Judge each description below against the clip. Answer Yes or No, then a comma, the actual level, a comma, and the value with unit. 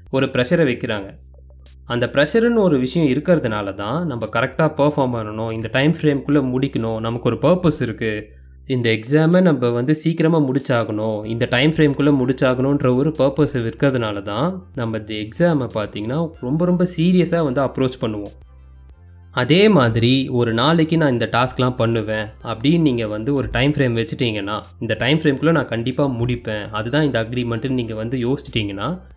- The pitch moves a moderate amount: Yes, average, 4.8 semitones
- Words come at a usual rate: No, fast, 150 wpm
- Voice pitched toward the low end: Yes, low, 125 Hz